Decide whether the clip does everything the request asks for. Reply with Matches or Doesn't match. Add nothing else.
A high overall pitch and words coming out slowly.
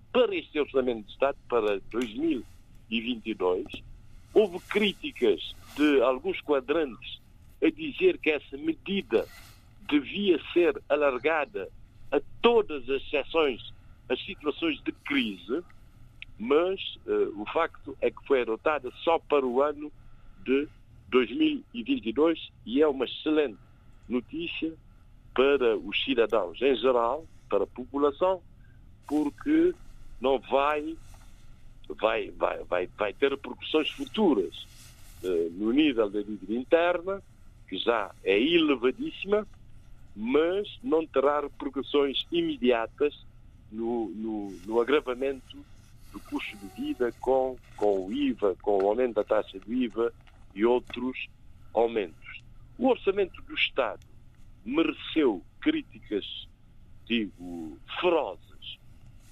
Doesn't match